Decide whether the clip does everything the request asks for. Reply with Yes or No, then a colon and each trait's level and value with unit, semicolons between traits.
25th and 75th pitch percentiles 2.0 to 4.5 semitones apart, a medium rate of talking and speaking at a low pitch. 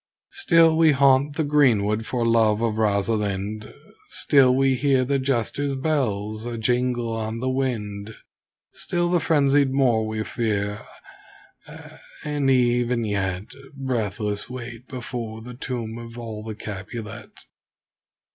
No: average, 3.7 semitones; slow, 125 wpm; low, 120 Hz